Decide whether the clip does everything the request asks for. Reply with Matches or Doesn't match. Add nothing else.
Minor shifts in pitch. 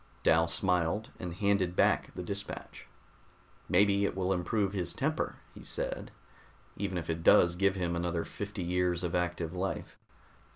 Matches